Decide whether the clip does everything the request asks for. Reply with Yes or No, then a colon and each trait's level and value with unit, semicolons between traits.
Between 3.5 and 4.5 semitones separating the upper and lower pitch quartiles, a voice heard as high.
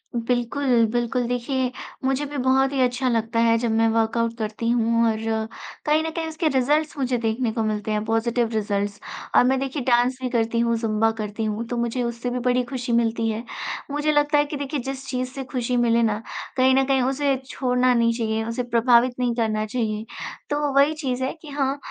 No: narrow, 2.6 semitones; high, 245 Hz